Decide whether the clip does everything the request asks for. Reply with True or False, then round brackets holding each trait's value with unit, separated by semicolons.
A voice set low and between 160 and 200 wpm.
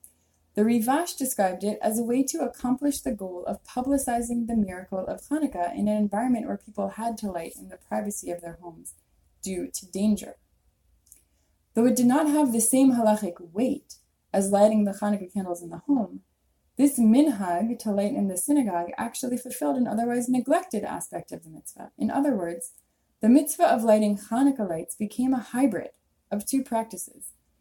False (215 Hz; 180 wpm)